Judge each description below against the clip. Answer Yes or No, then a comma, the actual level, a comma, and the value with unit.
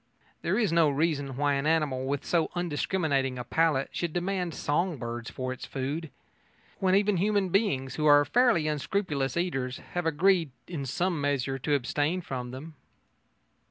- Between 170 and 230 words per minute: No, average, 160 wpm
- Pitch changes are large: No, average, 4.5 semitones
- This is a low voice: No, medium, 150 Hz